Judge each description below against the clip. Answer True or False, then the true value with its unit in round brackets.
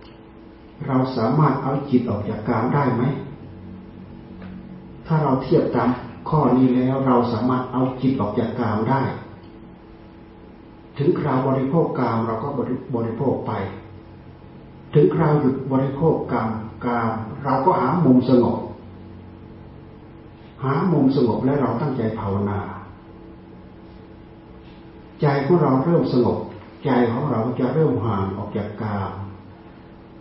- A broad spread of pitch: False (3.6 semitones)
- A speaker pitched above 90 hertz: True (120 Hz)